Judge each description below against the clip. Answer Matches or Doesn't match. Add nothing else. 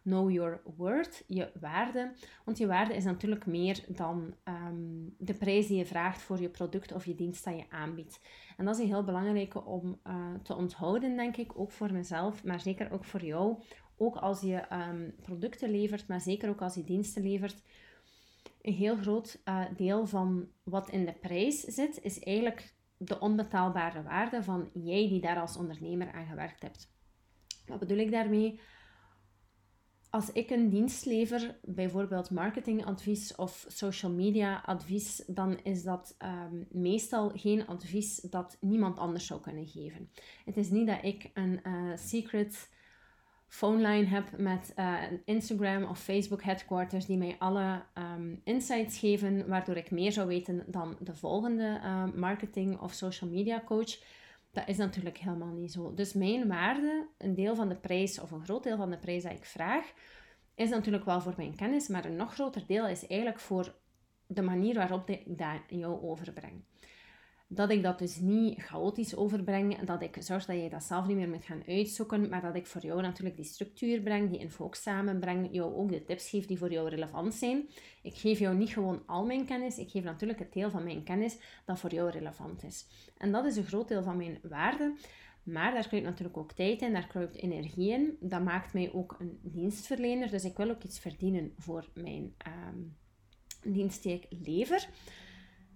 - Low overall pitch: Doesn't match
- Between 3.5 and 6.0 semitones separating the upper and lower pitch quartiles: Doesn't match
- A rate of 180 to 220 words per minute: Matches